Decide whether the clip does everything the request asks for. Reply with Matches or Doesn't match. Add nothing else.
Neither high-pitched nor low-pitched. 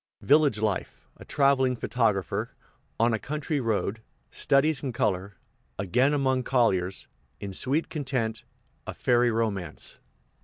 Doesn't match